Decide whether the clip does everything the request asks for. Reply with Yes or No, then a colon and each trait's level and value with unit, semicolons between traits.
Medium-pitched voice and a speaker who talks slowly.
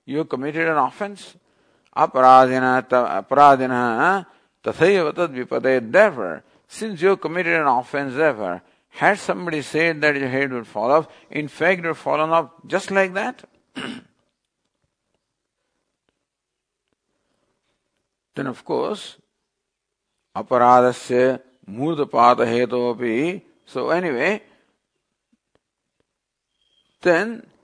Yes: medium, 145 Hz; slow, 80 wpm